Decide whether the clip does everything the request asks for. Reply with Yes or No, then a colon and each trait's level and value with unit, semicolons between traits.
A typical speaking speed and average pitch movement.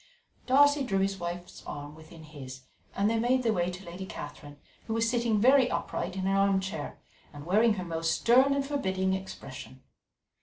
No: average, 180 wpm; wide, 5.9 semitones